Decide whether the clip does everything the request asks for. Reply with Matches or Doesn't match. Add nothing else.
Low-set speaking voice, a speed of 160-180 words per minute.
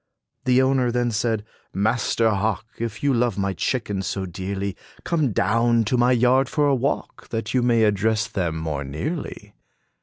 Matches